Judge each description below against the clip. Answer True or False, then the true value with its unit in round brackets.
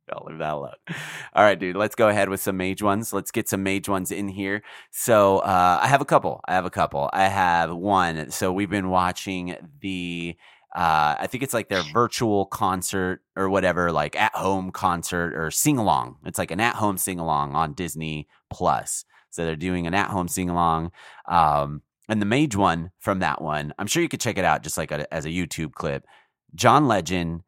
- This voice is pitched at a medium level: False (95 Hz)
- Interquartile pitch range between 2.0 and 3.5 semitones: True (3.1 semitones)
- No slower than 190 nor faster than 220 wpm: True (200 wpm)